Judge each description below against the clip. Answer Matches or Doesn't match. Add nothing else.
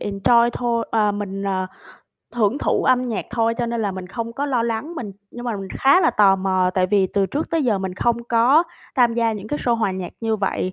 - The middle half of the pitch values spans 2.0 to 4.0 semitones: Matches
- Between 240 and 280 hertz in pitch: Doesn't match